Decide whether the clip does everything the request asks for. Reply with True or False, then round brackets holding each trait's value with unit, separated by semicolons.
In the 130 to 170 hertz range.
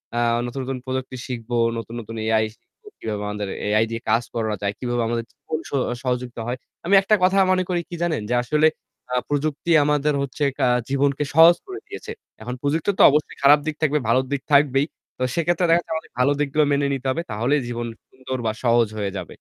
True (135 Hz)